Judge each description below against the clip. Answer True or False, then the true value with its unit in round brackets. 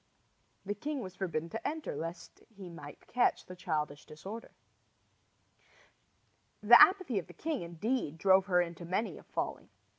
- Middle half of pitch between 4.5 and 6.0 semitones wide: True (5.4 semitones)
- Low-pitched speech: False (190 Hz)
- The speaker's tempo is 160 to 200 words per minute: False (150 wpm)